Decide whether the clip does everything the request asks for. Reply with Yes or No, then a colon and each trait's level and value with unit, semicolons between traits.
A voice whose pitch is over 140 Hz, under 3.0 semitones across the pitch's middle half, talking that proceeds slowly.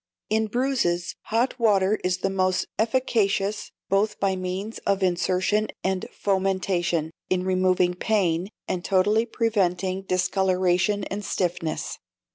Yes: high, 190 Hz; narrow, 2.4 semitones; slow, 115 wpm